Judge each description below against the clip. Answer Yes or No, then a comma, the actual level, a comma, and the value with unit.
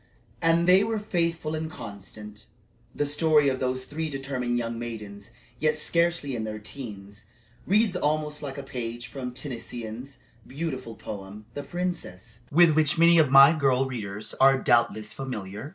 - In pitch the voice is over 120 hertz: Yes, low, 135 Hz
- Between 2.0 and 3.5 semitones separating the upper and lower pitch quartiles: No, wide, 5.4 semitones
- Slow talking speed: No, average, 150 wpm